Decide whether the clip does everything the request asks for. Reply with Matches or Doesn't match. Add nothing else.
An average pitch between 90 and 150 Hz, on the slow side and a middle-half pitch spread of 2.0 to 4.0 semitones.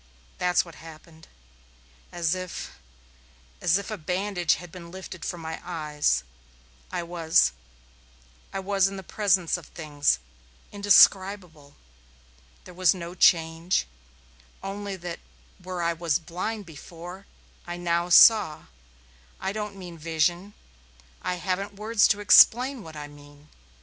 Doesn't match